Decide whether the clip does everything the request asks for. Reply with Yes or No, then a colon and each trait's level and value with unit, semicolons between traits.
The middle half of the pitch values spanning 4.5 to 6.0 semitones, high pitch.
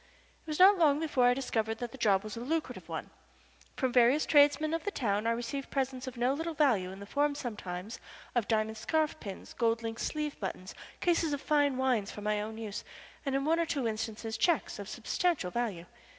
Yes: average, 5.2 semitones; high, 245 Hz